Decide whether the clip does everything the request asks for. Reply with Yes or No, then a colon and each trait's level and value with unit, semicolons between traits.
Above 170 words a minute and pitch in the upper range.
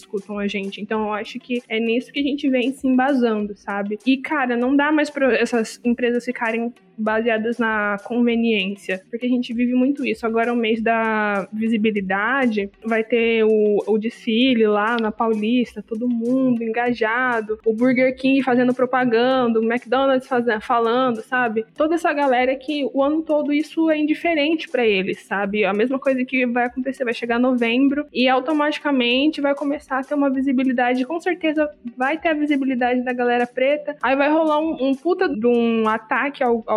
Yes: average, 180 wpm; high, 245 Hz